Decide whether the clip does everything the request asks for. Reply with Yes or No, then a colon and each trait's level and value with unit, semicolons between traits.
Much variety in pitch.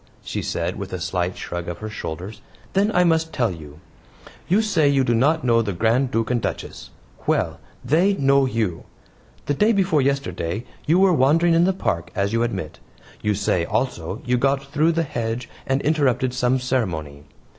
Yes: wide, 6.8 semitones